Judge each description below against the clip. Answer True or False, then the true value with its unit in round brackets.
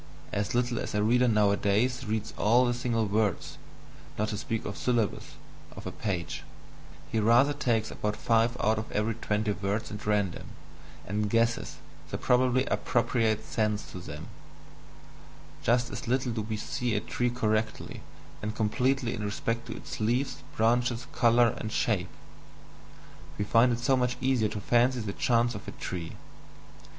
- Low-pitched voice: True (115 Hz)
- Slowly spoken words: False (160 wpm)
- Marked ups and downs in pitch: False (2.6 semitones)